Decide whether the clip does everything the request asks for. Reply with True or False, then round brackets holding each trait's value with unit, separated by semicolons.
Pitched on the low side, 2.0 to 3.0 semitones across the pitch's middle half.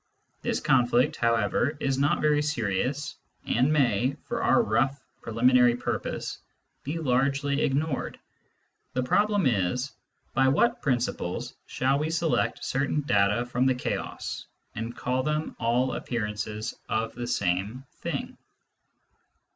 False (130 Hz; 3.4 semitones)